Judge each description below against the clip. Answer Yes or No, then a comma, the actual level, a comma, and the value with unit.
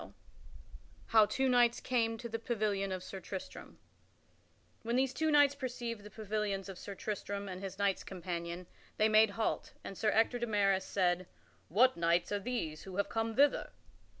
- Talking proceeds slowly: No, average, 175 wpm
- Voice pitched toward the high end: Yes, high, 210 Hz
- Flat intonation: No, average, 3.4 semitones